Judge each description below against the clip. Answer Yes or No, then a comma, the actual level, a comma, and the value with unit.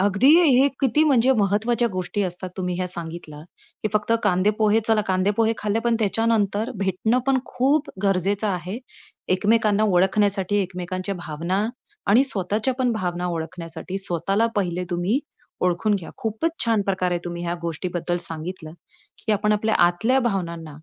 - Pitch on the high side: Yes, high, 195 Hz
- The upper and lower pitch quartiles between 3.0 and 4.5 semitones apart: Yes, average, 3.6 semitones